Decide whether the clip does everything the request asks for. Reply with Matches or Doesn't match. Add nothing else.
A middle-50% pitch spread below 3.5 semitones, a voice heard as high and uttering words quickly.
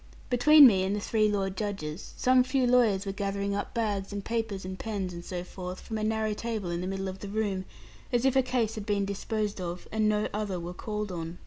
Matches